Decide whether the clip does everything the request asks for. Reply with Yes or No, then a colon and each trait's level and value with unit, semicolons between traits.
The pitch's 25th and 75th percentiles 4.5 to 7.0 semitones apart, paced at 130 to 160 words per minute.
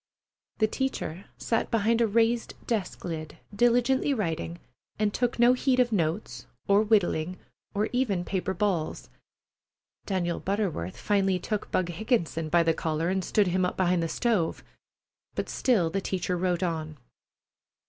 Yes: average, 4.8 semitones; average, 150 wpm